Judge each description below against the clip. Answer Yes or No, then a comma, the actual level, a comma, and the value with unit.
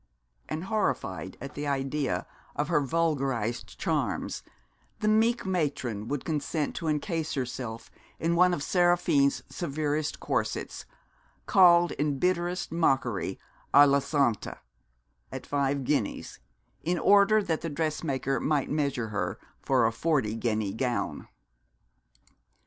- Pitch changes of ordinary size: Yes, average, 4.2 semitones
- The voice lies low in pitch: No, medium, 145 Hz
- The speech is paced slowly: Yes, slow, 120 wpm